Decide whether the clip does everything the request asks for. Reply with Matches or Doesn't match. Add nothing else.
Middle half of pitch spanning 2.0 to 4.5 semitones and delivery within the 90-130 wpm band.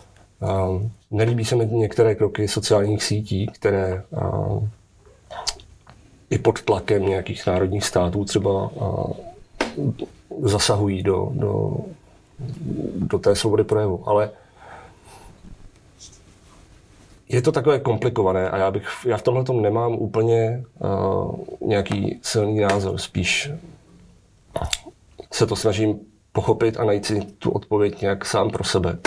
Matches